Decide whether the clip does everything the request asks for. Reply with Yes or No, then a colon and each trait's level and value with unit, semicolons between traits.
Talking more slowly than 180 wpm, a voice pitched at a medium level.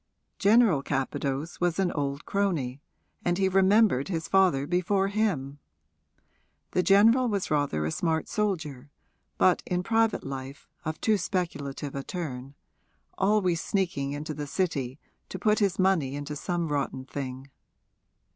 Yes: slow, 135 wpm; medium, 165 Hz